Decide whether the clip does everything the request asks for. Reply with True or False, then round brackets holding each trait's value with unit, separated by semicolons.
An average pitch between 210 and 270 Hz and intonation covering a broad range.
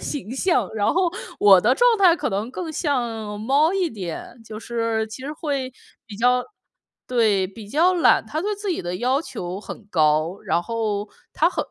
True (235 Hz; 7.1 semitones)